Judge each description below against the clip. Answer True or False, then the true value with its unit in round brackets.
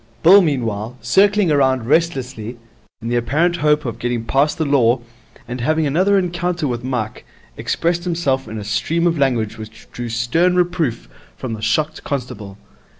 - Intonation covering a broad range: True (6.2 semitones)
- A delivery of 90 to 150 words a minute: False (160 wpm)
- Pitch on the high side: False (135 Hz)